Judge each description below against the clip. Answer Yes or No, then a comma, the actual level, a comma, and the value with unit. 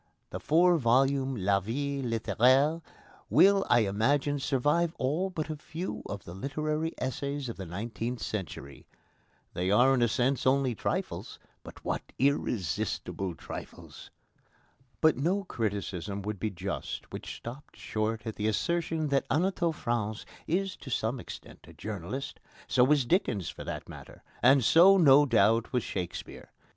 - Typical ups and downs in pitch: No, wide, 5.7 semitones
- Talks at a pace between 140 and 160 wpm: Yes, average, 150 wpm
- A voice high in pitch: No, low, 130 Hz